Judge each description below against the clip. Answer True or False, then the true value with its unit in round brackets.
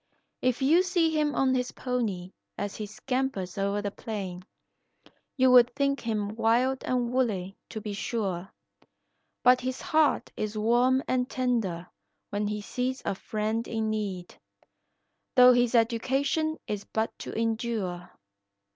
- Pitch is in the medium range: False (230 Hz)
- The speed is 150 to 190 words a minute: False (140 wpm)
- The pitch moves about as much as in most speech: True (3.7 semitones)